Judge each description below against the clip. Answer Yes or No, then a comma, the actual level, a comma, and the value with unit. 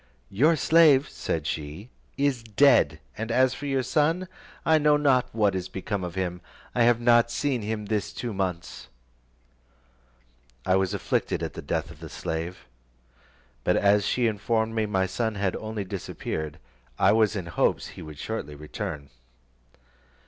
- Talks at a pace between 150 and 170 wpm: Yes, average, 160 wpm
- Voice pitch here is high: No, low, 110 Hz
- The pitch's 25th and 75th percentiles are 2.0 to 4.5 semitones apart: No, average, 5.0 semitones